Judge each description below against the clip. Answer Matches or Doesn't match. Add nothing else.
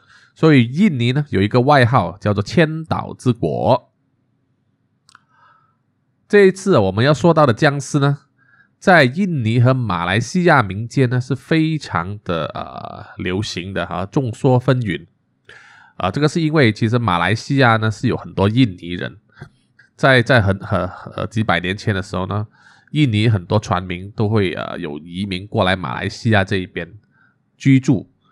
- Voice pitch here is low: Matches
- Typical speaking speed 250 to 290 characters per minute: Doesn't match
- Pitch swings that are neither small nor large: Doesn't match